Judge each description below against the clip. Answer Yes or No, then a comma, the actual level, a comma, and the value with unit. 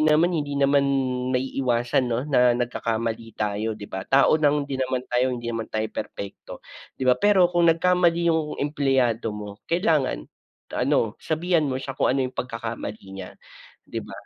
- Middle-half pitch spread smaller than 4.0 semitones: No, average, 4.8 semitones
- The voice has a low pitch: Yes, low, 130 Hz